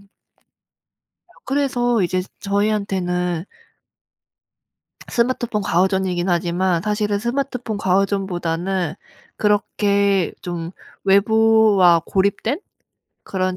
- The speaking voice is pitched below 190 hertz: No, high, 195 Hz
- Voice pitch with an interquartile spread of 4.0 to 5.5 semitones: No, average, 3.1 semitones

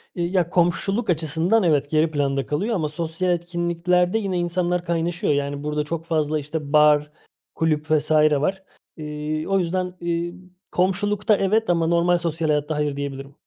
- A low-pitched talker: No, medium, 165 Hz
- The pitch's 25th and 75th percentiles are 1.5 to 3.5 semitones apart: Yes, average, 2.9 semitones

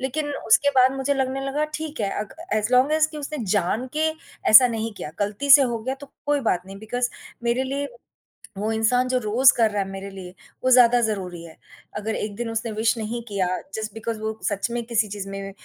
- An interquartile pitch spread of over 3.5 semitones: Yes, average, 4.0 semitones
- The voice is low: No, high, 230 Hz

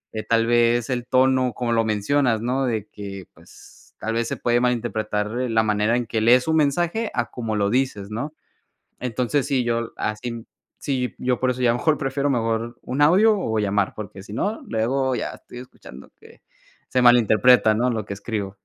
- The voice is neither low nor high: No, low, 120 Hz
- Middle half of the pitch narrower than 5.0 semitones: Yes, average, 2.7 semitones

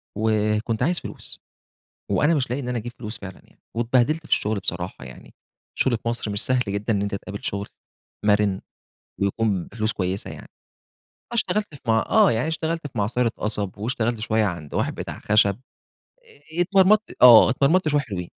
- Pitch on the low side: Yes, low, 110 Hz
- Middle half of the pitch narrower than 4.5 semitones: Yes, average, 4.0 semitones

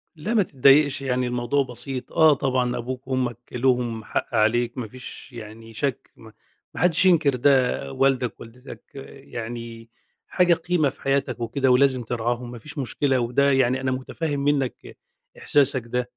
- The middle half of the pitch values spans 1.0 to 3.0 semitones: Yes, narrow, 2.6 semitones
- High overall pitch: No, low, 130 Hz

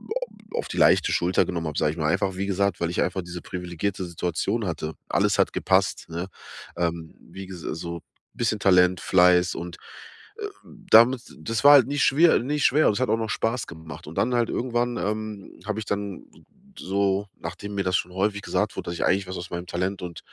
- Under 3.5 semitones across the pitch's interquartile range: No, average, 3.9 semitones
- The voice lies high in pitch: No, very low, 95 Hz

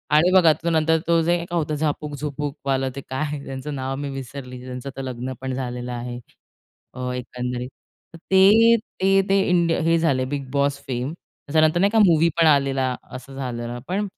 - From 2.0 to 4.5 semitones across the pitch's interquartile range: Yes, average, 4.0 semitones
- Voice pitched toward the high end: No, medium, 140 Hz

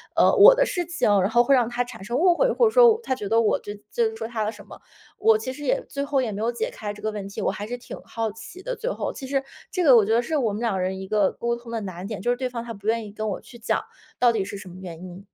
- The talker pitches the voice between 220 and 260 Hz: Yes, high, 230 Hz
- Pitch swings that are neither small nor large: Yes, average, 3.9 semitones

